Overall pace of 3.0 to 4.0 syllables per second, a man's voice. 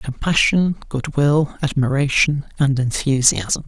Yes: 3.9 syllables/s; male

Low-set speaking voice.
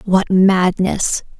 No: high, 190 Hz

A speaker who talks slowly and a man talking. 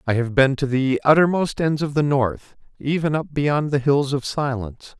No: fast, 205 wpm; male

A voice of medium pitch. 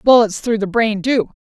No: high, 220 Hz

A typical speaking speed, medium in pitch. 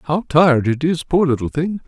No: fast, 225 wpm; medium, 150 Hz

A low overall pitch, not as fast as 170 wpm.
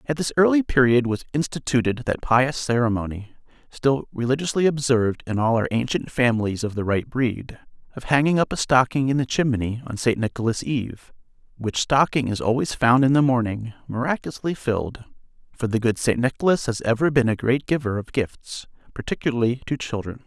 No: low, 125 Hz; average, 175 wpm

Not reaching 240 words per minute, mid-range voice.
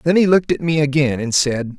No: fast, 270 wpm; medium, 145 Hz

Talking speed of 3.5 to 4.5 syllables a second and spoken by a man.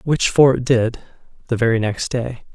Yes: 4.3 syllables/s; male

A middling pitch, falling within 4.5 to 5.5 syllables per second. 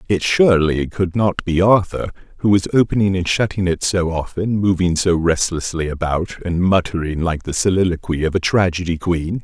No: very low, 90 Hz; 5.1 syllables/s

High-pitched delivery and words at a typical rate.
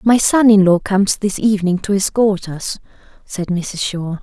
Yes: high, 195 Hz; average, 185 wpm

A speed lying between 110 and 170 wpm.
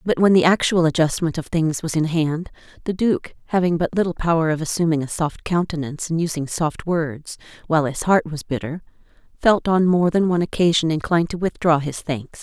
No: average, 200 wpm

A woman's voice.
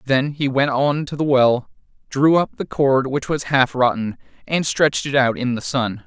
No: male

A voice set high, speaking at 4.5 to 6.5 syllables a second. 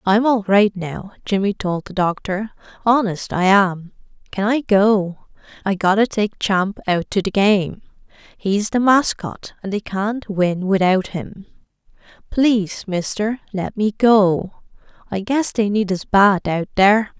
No: high, 200 Hz; 3.9 syllables/s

